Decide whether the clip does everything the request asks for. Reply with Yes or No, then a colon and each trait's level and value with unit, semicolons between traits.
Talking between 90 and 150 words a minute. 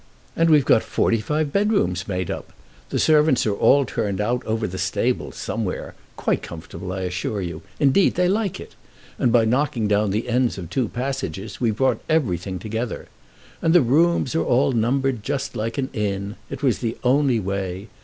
No: average, 185 wpm